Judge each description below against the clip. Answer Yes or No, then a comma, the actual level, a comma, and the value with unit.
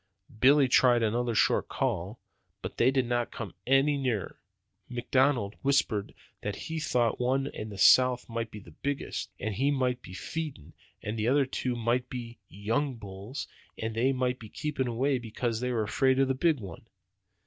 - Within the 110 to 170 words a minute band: No, average, 185 wpm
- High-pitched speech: No, low, 125 Hz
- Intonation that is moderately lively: Yes, average, 3.3 semitones